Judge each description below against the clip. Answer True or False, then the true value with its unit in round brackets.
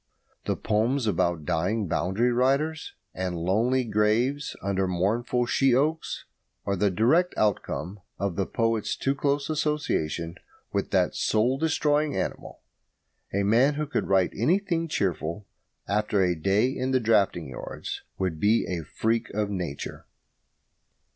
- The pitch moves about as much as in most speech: False (6.1 semitones)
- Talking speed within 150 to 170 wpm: False (135 wpm)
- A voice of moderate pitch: False (110 Hz)